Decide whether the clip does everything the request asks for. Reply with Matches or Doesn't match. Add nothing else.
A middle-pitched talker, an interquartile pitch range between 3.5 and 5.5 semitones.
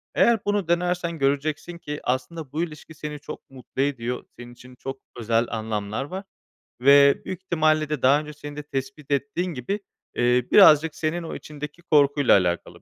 Matches